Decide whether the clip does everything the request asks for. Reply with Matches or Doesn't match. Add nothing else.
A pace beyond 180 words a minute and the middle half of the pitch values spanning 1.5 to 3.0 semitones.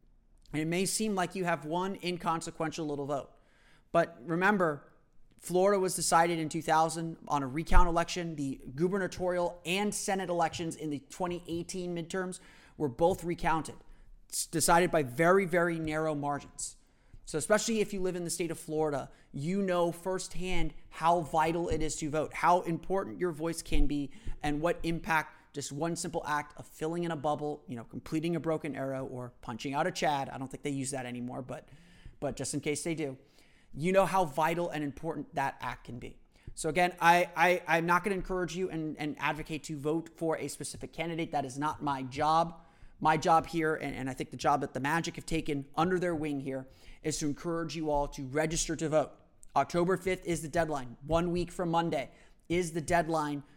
Matches